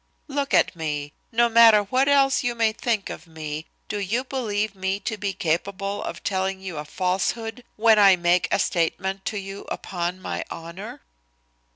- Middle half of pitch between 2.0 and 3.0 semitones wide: No, average, 3.9 semitones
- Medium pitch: No, high, 195 Hz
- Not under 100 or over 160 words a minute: No, average, 175 wpm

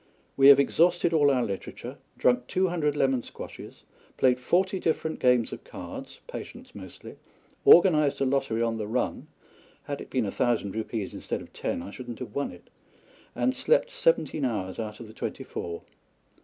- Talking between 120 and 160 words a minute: No, average, 180 wpm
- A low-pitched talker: Yes, low, 130 Hz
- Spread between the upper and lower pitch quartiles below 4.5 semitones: No, wide, 5.6 semitones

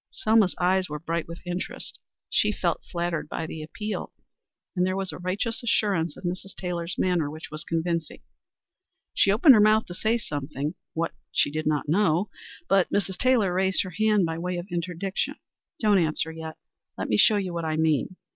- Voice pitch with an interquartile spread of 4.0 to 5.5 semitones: No, average, 3.3 semitones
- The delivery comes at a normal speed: Yes, average, 190 wpm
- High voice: No, medium, 180 Hz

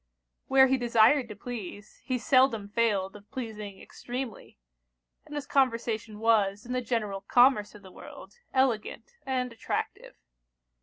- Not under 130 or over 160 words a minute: Yes, average, 140 wpm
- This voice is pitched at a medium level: No, high, 230 Hz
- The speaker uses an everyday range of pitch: Yes, average, 3.5 semitones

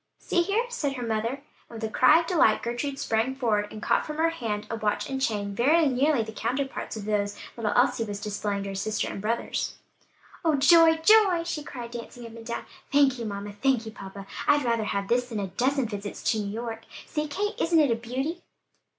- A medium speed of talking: No, fast, 220 wpm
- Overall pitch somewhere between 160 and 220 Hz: No, high, 235 Hz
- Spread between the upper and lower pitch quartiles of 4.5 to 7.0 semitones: Yes, average, 5.1 semitones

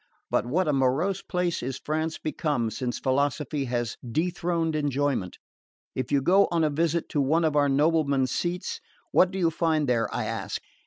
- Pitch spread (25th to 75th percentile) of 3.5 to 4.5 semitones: Yes, average, 3.9 semitones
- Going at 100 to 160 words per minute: No, average, 175 wpm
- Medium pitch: Yes, medium, 150 Hz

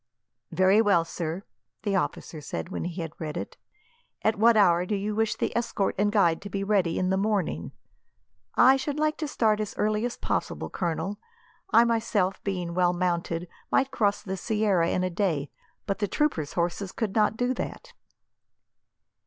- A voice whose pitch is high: Yes, high, 195 Hz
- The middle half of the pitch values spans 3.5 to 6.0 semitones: Yes, average, 3.8 semitones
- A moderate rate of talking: Yes, average, 180 wpm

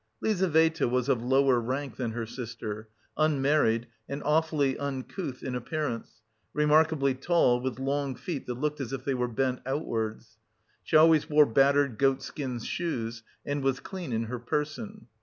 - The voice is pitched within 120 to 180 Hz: Yes, low, 135 Hz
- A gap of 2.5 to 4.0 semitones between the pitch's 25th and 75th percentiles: Yes, average, 3.6 semitones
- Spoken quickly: No, average, 155 wpm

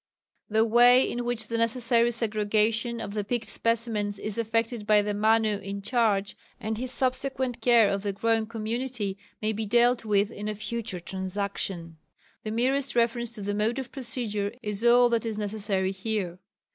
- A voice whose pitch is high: Yes, high, 220 Hz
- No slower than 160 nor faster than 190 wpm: Yes, average, 170 wpm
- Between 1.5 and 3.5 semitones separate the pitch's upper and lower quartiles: Yes, narrow, 2.5 semitones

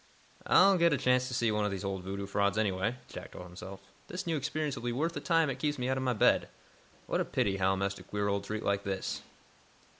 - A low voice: Yes, low, 110 Hz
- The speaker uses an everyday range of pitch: No, wide, 5.8 semitones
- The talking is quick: Yes, fast, 250 wpm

